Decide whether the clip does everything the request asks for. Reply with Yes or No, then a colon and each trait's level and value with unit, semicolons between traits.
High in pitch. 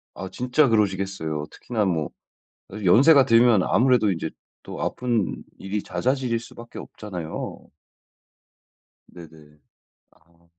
No: low, 105 Hz